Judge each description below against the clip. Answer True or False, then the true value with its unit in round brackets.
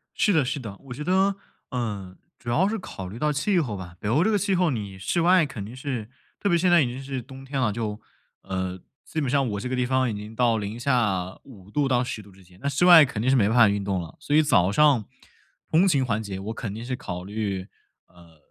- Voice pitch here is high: False (120 Hz)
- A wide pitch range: True (6.1 semitones)